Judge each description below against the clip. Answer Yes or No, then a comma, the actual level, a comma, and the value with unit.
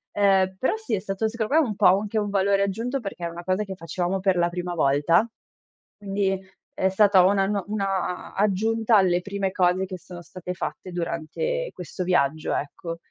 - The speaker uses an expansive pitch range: No, narrow, 2.5 semitones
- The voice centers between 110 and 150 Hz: No, high, 190 Hz